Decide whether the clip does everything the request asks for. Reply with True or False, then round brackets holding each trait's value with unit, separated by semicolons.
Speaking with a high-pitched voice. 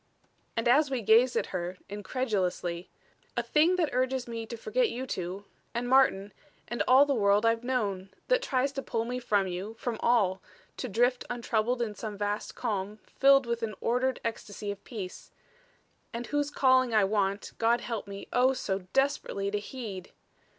True (230 Hz)